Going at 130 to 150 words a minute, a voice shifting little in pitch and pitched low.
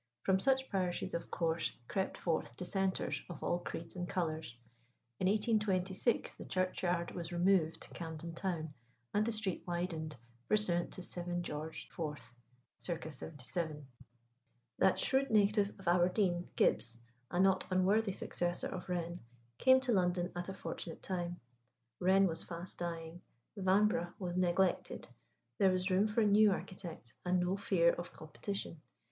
No: average, 145 wpm; narrow, 2.2 semitones; medium, 180 Hz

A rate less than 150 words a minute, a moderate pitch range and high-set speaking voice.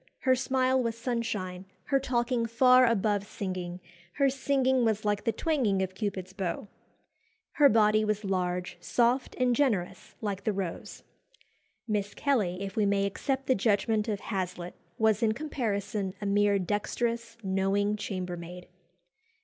Yes: average, 140 wpm; average, 3.7 semitones; high, 210 Hz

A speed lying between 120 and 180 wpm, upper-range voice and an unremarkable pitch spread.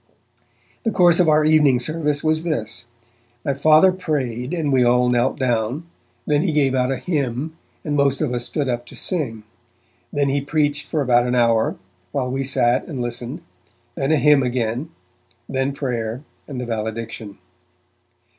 No: average, 165 wpm; low, 135 Hz; average, 3.9 semitones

